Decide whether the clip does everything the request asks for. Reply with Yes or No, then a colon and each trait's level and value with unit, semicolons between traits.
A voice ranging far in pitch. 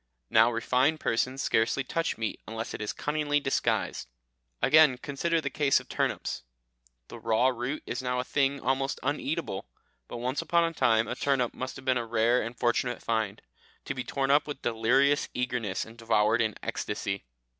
No: average, 3.5 semitones